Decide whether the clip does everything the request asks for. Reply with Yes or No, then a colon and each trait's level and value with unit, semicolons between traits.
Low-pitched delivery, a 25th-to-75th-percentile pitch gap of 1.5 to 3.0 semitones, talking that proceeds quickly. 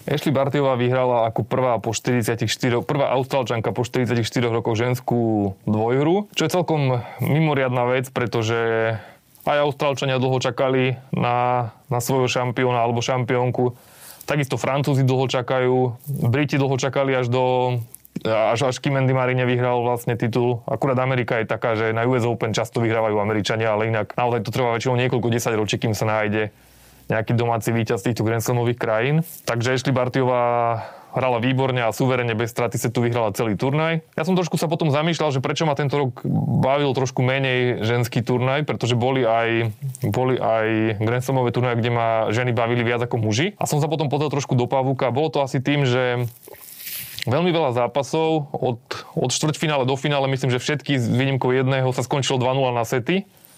Yes: low, 125 Hz; narrow, 2.5 semitones; fast, 170 wpm